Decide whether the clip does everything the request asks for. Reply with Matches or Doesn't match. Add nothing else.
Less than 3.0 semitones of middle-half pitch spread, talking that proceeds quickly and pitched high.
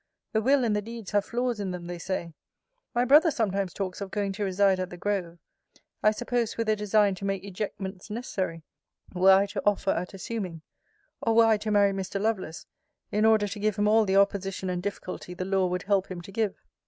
Matches